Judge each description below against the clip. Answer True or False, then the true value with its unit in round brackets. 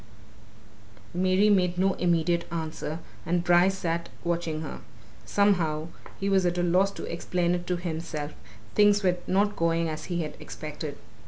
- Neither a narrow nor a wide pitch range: False (2.0 semitones)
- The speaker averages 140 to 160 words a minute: True (155 wpm)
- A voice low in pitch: False (175 Hz)